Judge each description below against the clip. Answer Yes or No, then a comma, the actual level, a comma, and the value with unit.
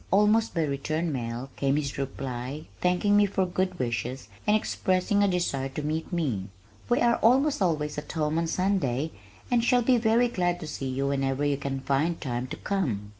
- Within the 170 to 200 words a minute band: Yes, average, 195 wpm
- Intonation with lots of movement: Yes, wide, 6.4 semitones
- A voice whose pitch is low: No, medium, 155 Hz